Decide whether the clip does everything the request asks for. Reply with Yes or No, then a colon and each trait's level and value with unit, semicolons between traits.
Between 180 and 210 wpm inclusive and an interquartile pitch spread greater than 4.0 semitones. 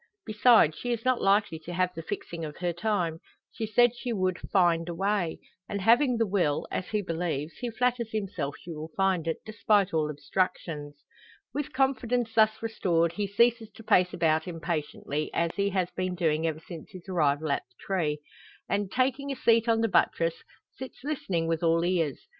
Yes: average, 190 wpm; average, 5.3 semitones